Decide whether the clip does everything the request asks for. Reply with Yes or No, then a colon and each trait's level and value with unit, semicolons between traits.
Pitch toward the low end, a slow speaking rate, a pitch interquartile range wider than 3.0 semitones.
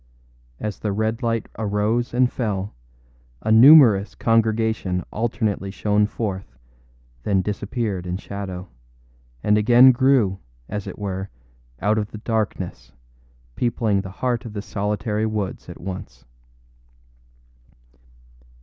No: low, 105 Hz; slow, 115 wpm; average, 2.7 semitones